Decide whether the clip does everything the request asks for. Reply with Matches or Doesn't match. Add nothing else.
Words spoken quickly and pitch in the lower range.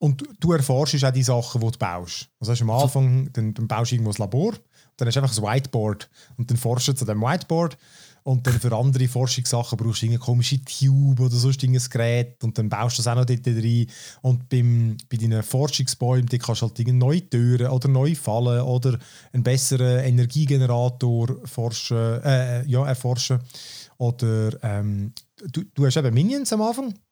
Matches